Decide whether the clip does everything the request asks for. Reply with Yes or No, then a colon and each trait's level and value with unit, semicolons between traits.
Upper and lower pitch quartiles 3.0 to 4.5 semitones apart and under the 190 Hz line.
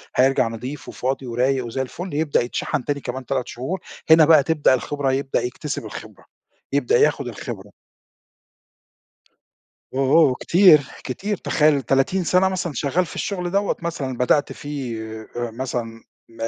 Yes: average, 4.1 semitones; low, 135 Hz